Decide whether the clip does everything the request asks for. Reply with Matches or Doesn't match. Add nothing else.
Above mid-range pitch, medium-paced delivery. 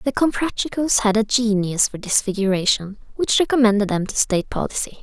Matches